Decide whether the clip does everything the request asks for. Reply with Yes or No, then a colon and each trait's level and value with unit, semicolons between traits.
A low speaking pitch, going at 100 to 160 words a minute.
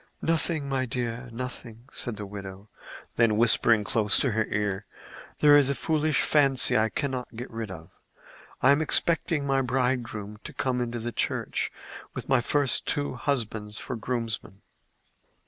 Yes: low, 120 Hz; average, 155 wpm